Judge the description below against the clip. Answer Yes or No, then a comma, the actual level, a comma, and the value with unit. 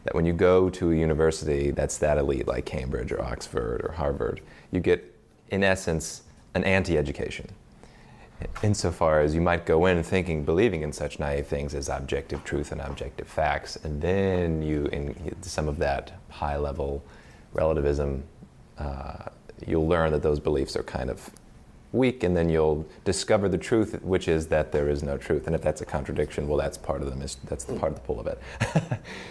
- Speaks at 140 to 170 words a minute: No, average, 185 wpm